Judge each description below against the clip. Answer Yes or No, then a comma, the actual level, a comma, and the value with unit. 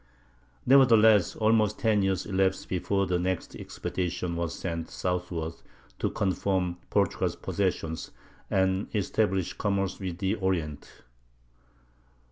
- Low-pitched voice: Yes, very low, 95 Hz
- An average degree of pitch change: No, narrow, 2.3 semitones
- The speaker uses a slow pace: Yes, slow, 105 wpm